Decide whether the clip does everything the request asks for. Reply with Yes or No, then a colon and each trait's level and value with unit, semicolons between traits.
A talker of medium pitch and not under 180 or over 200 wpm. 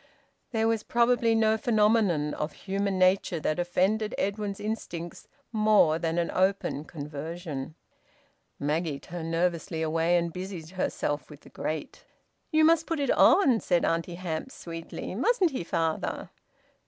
No: medium, 180 Hz; average, 140 wpm